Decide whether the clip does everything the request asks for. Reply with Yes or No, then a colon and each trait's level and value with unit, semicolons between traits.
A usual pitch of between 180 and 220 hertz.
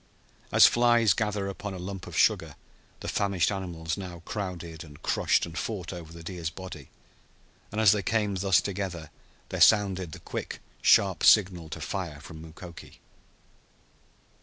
No: very low, 95 Hz